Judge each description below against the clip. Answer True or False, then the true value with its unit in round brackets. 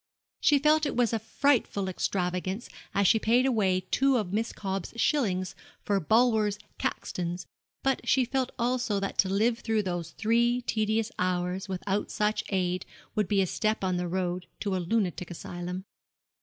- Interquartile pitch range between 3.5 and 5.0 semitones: True (4.1 semitones)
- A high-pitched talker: True (205 Hz)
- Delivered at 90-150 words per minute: False (165 wpm)